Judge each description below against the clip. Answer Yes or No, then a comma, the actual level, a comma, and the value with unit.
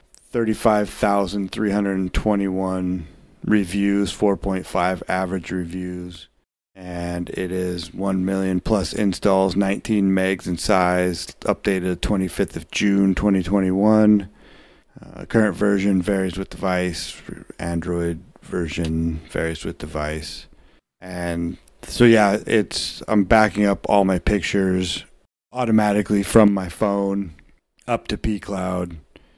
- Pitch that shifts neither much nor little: No, narrow, 2.3 semitones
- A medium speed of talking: No, slow, 100 wpm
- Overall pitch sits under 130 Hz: Yes, very low, 95 Hz